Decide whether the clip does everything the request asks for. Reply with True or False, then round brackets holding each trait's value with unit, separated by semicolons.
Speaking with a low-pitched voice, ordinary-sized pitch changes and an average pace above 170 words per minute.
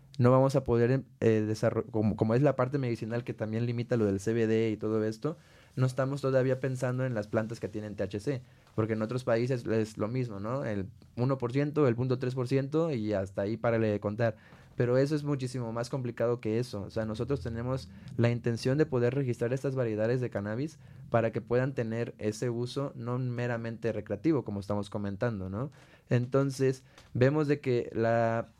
True (120 Hz; 3.0 semitones; 185 wpm)